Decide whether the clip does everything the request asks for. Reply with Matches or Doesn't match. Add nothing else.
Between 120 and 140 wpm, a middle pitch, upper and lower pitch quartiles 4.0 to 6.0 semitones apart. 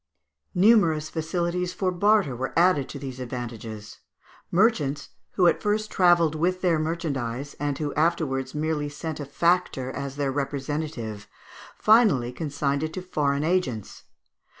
Matches